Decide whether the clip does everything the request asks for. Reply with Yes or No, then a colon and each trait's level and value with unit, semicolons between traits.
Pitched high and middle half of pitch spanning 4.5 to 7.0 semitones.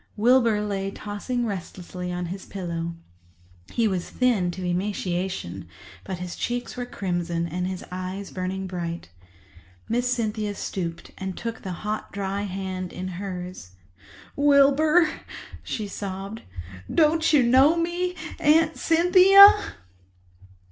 Yes: high, 200 Hz; wide, 5.6 semitones